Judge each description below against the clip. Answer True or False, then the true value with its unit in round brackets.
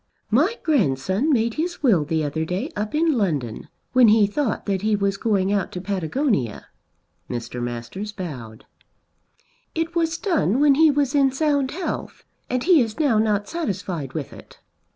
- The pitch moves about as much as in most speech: False (8.3 semitones)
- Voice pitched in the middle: False (215 Hz)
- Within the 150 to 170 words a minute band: True (165 wpm)